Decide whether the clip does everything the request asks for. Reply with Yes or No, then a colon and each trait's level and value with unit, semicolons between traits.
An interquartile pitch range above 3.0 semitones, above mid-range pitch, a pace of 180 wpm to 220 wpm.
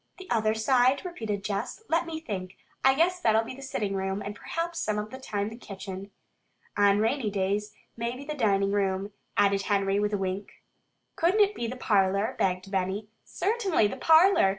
Yes: average, 5.2 semitones; high, 210 Hz; average, 185 wpm